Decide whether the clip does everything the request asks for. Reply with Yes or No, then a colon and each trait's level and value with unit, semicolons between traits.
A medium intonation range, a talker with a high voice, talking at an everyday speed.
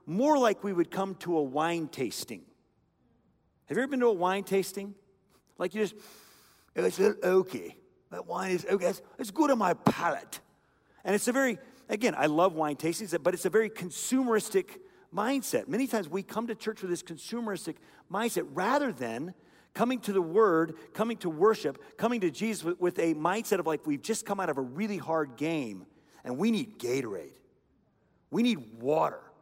Yes: average, 4.5 semitones; high, 200 Hz; average, 190 wpm